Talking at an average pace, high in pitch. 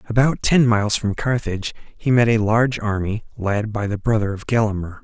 No: average, 190 wpm; low, 110 Hz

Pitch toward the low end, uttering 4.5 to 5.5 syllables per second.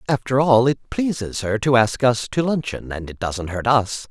Yes: low, 120 Hz; 4.6 syllables/s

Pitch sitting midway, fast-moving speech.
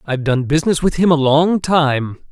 Yes: medium, 150 Hz; fast, 210 wpm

